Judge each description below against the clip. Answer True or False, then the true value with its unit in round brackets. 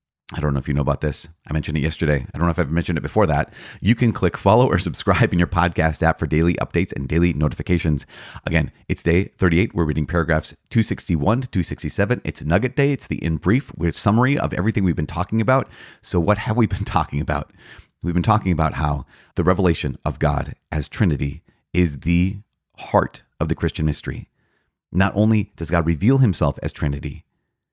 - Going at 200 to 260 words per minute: True (205 wpm)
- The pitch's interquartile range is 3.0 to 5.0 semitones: True (4.3 semitones)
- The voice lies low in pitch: True (85 Hz)